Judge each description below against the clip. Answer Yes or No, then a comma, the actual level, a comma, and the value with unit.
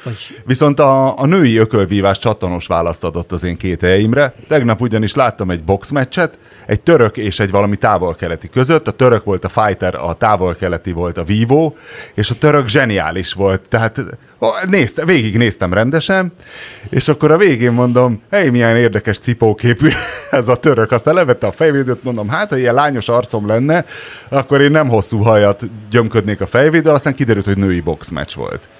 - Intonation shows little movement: No, average, 5.2 semitones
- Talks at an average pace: No, fast, 165 wpm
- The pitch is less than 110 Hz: No, low, 115 Hz